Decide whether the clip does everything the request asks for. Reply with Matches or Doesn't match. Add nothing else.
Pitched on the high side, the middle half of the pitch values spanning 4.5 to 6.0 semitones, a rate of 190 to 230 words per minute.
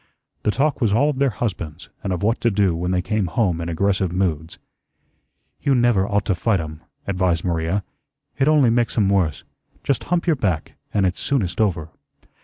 Doesn't match